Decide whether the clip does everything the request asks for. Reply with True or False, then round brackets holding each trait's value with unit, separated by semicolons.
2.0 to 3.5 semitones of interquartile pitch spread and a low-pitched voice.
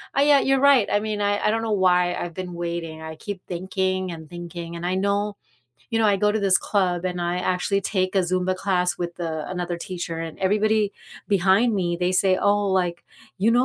False (2.7 semitones; 185 Hz)